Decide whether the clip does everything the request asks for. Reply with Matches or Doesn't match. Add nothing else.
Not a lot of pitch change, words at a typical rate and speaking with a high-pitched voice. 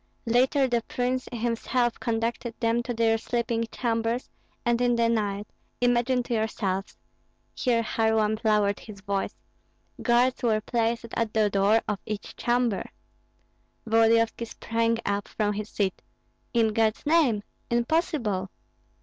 Doesn't match